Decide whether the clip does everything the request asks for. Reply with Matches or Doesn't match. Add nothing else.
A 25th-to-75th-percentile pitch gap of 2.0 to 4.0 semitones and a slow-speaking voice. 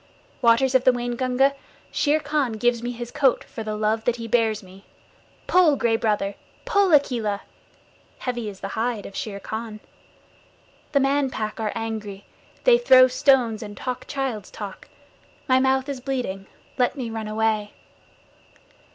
Doesn't match